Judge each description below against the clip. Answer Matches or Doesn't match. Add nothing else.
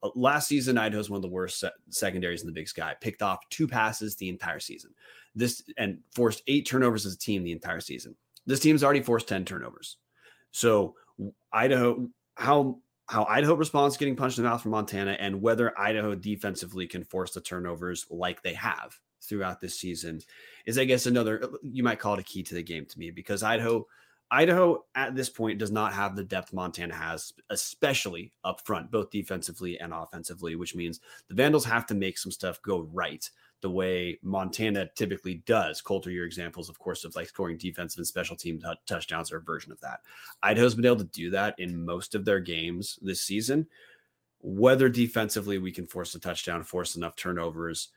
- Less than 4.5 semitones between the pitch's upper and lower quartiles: Doesn't match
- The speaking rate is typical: Matches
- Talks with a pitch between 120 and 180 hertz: Doesn't match